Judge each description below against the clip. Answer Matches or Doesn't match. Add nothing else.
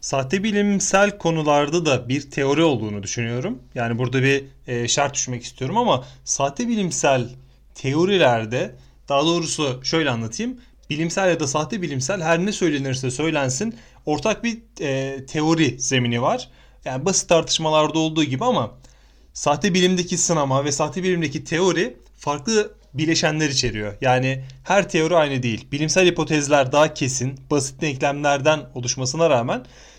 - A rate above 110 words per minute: Matches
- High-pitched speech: Doesn't match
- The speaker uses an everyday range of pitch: Matches